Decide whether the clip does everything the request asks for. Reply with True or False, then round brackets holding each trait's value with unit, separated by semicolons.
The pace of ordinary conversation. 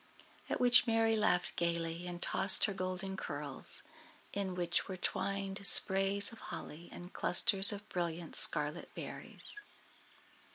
False (130 wpm)